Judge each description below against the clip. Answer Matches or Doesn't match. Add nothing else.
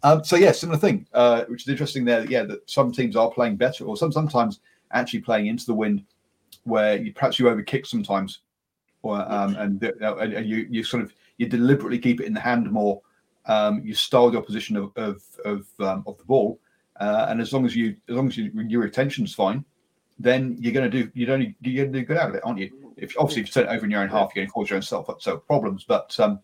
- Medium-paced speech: Doesn't match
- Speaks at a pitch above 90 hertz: Matches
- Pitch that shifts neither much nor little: Matches